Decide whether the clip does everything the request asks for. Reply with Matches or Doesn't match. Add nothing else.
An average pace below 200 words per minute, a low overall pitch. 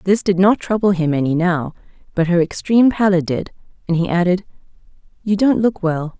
Doesn't match